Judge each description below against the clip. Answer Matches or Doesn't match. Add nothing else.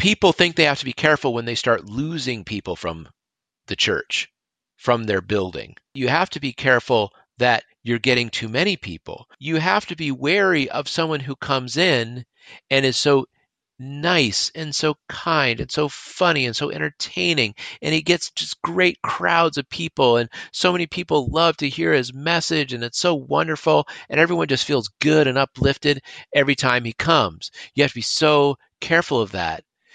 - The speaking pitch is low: Doesn't match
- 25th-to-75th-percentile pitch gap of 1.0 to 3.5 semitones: Doesn't match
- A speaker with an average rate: Matches